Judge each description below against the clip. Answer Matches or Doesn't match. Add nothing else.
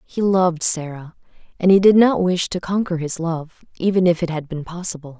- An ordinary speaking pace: Matches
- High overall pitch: Doesn't match